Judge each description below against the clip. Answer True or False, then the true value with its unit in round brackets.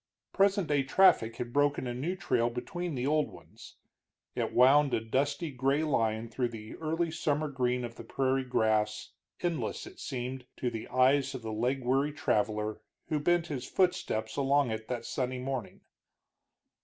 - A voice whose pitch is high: False (130 Hz)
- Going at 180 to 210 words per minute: False (165 wpm)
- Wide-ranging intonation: False (3.7 semitones)